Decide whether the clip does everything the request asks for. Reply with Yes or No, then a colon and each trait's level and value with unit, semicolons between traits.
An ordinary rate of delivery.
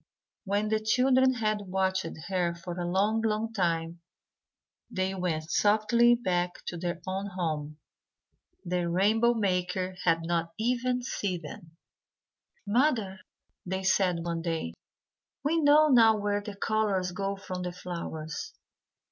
No: slow, 130 wpm